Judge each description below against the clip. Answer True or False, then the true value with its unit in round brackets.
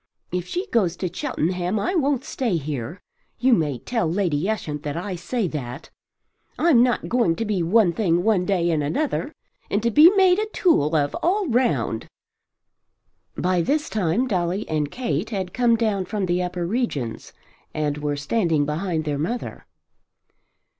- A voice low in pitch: False (185 Hz)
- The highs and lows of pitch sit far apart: True (6.9 semitones)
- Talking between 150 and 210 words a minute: True (165 wpm)